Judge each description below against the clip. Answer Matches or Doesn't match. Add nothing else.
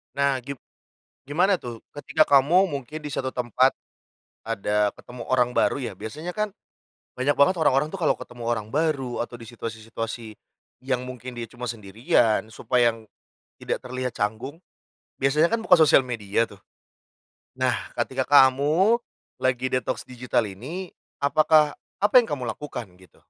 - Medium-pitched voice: Doesn't match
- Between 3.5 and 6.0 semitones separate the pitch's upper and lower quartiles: Matches